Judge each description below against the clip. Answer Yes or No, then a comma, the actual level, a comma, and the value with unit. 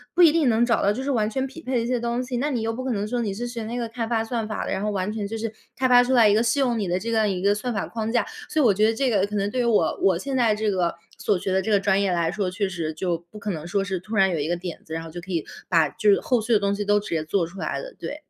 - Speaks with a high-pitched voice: Yes, high, 215 Hz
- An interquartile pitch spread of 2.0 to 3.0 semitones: No, average, 3.8 semitones